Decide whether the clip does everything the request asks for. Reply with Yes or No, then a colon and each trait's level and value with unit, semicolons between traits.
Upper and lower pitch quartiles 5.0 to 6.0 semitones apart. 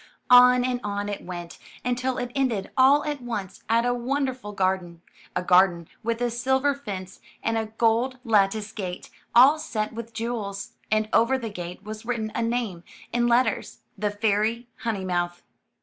No: average, 3.6 semitones